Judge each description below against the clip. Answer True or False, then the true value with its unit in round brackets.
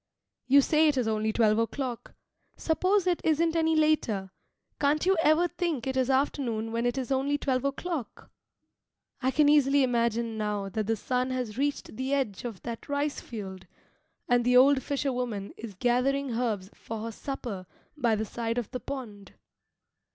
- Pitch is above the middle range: True (250 Hz)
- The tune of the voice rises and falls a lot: False (4.0 semitones)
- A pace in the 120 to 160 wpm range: False (175 wpm)